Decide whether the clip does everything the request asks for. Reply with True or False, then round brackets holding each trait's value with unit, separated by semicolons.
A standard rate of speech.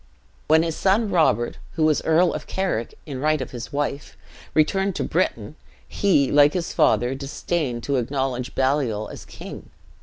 True (160 wpm)